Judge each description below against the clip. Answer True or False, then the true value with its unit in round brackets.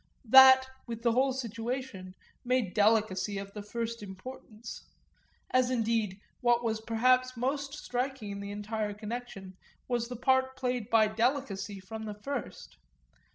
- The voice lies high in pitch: True (230 Hz)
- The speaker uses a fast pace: False (140 wpm)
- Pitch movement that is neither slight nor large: True (3.4 semitones)